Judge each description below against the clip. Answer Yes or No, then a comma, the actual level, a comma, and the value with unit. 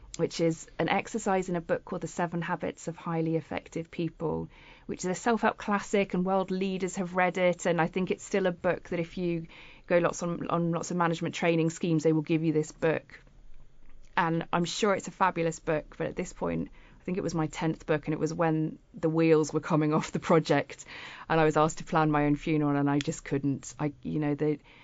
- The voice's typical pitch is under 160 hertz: No, medium, 165 Hz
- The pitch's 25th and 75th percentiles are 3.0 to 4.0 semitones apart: No, narrow, 2.5 semitones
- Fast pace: Yes, fast, 235 wpm